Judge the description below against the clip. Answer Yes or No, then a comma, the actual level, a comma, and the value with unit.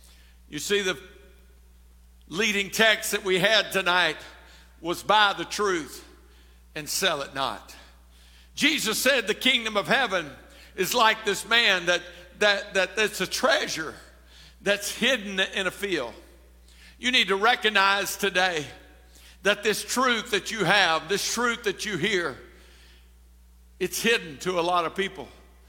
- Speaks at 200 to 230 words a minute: No, average, 140 wpm